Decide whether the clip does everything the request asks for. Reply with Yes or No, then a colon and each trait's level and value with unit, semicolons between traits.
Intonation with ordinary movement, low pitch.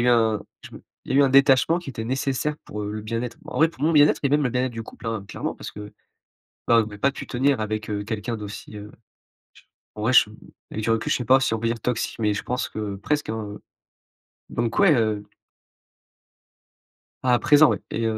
Yes: average, 3.7 semitones; low, 115 Hz